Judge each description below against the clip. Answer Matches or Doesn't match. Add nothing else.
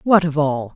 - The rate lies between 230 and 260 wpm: Matches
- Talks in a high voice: Doesn't match